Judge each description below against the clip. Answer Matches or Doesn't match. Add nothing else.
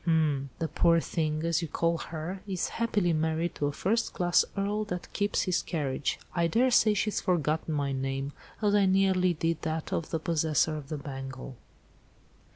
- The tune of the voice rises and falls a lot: Doesn't match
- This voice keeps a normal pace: Matches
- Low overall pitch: Doesn't match